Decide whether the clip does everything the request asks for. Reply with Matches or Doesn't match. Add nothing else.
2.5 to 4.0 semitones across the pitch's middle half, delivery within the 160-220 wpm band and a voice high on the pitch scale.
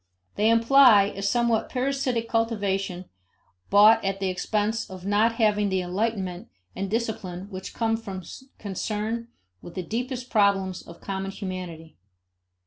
Doesn't match